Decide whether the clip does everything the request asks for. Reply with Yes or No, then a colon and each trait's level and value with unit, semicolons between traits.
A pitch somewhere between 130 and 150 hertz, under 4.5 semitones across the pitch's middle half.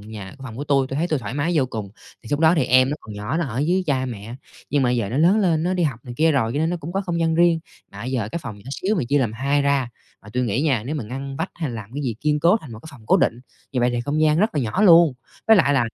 No: medium, 140 Hz; average, 5.0 semitones